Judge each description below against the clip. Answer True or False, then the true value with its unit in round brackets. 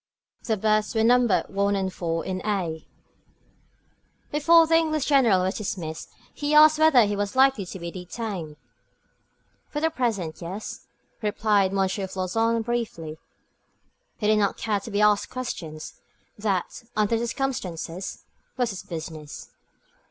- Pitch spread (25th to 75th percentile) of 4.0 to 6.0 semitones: True (4.4 semitones)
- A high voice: True (210 Hz)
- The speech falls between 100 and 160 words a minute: True (140 wpm)